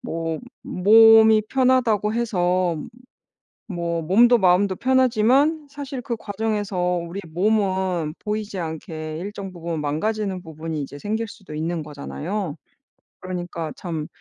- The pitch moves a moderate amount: Yes, average, 4.8 semitones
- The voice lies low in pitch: No, high, 190 Hz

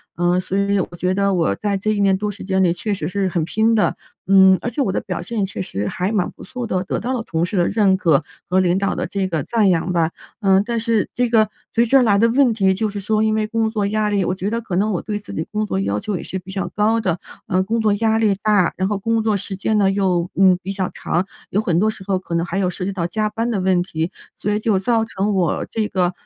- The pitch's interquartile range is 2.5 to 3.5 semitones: Yes, average, 2.9 semitones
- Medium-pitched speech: No, high, 195 Hz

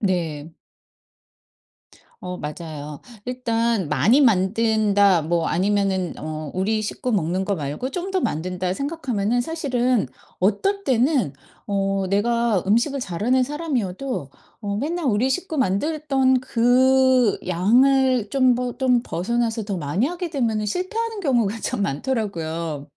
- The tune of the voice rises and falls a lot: Yes, wide, 5.9 semitones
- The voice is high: Yes, high, 225 Hz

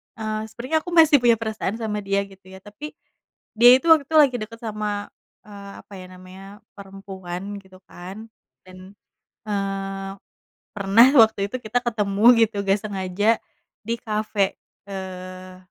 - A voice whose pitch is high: Yes, high, 205 Hz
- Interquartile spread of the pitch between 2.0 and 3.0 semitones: Yes, average, 2.7 semitones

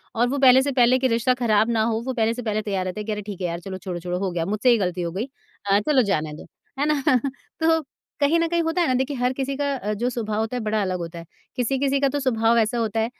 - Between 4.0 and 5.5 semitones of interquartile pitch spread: Yes, average, 4.7 semitones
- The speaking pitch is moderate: No, high, 230 Hz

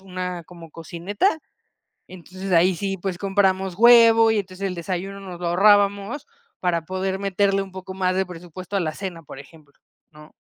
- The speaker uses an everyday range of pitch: No, narrow, 2.1 semitones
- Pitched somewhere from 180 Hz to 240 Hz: Yes, medium, 185 Hz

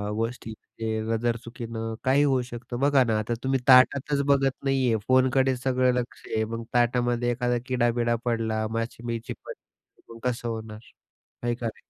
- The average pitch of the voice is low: Yes, low, 120 Hz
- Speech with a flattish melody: Yes, narrow, 2.1 semitones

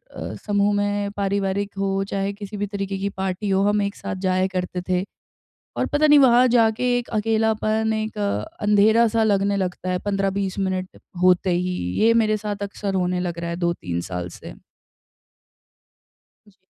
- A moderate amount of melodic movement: No, narrow, 2.3 semitones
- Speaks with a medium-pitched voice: No, high, 200 Hz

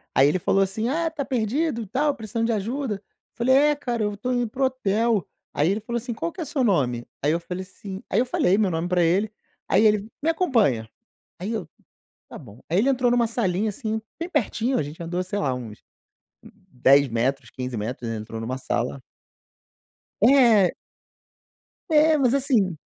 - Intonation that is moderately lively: No, wide, 7.3 semitones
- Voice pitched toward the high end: Yes, high, 210 Hz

